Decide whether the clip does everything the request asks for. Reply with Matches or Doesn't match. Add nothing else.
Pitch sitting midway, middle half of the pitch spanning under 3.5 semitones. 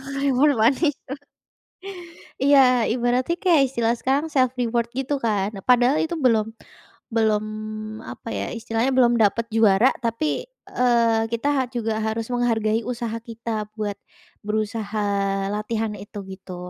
Doesn't match